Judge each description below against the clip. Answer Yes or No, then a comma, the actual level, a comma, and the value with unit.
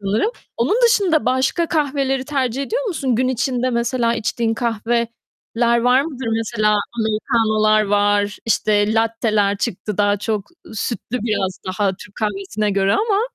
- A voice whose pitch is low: No, high, 230 Hz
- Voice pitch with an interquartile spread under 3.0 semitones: No, average, 3.6 semitones